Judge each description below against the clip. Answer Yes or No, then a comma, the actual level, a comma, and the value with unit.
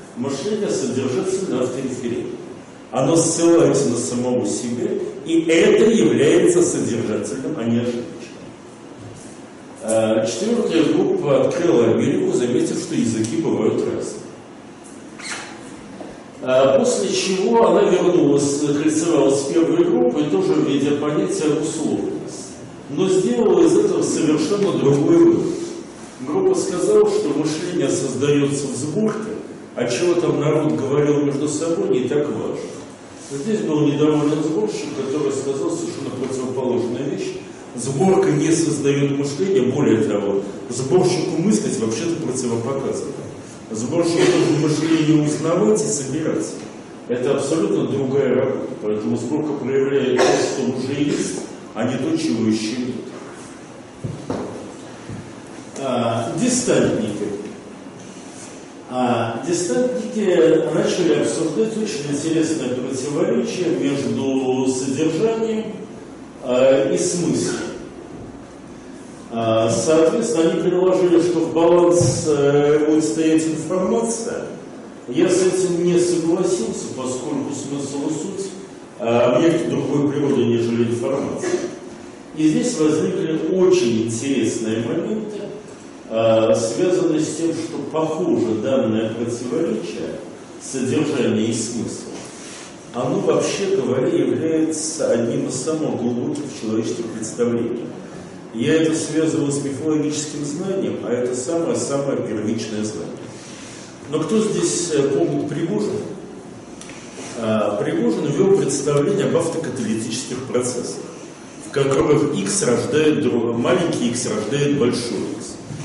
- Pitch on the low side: No, medium, 150 Hz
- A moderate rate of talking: No, slow, 105 wpm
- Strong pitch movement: Yes, wide, 6.0 semitones